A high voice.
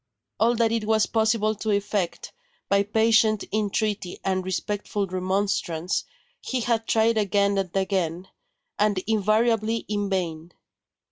Yes: high, 205 Hz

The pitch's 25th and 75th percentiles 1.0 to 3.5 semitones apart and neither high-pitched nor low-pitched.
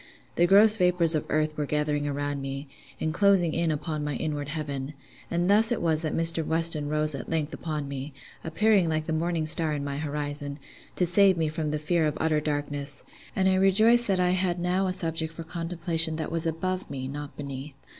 Yes: average, 2.9 semitones; medium, 160 Hz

